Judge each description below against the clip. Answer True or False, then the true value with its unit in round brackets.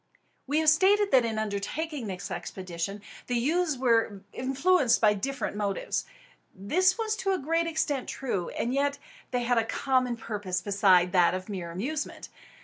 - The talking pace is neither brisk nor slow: True (160 wpm)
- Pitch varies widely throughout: True (7.2 semitones)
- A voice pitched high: True (240 Hz)